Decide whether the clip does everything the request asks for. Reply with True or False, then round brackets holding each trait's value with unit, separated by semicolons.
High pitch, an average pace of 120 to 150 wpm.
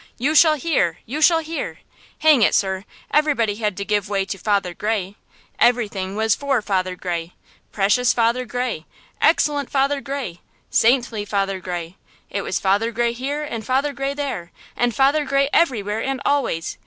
False (230 Hz; 165 wpm)